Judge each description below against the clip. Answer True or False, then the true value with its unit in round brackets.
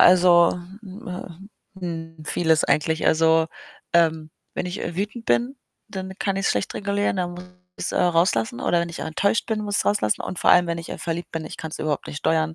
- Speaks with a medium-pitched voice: True (175 Hz)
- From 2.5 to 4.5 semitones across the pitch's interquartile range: True (2.9 semitones)